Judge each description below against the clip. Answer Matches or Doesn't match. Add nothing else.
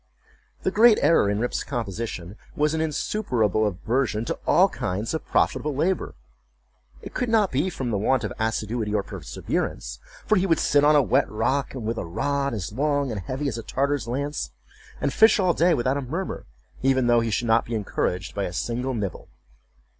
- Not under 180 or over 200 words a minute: Matches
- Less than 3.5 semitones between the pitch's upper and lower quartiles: Doesn't match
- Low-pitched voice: Matches